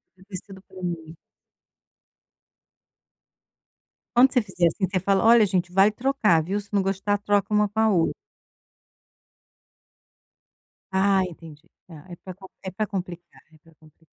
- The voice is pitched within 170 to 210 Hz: Yes, high, 190 Hz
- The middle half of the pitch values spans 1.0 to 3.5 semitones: Yes, average, 2.9 semitones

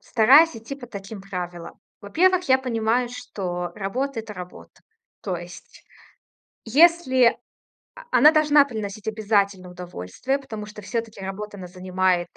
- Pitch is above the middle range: Yes, high, 215 Hz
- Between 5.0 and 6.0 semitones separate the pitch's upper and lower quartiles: Yes, wide, 5.6 semitones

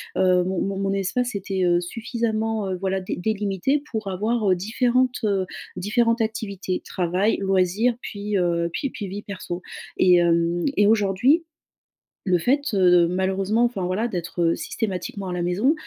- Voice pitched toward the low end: No, high, 195 Hz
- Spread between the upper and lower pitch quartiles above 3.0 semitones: Yes, average, 3.4 semitones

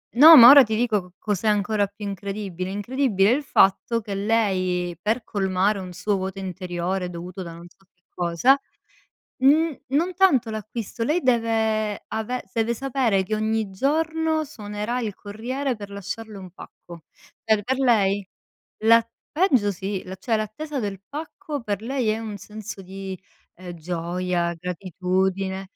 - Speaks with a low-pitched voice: No, high, 210 Hz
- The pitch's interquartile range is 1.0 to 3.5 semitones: No, average, 4.1 semitones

